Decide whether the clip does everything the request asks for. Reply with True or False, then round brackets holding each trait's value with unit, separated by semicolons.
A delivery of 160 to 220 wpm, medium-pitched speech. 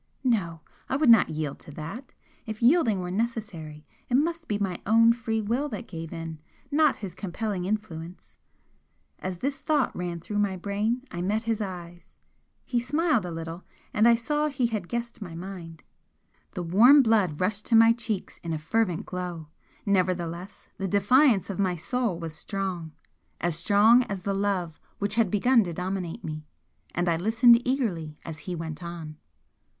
False (175 wpm; 195 Hz)